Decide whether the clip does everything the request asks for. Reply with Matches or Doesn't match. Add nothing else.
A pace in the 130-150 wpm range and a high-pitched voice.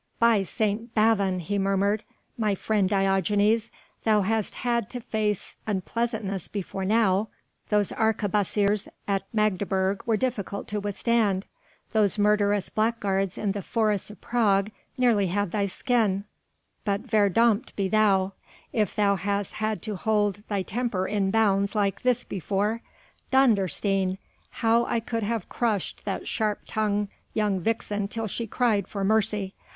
Matches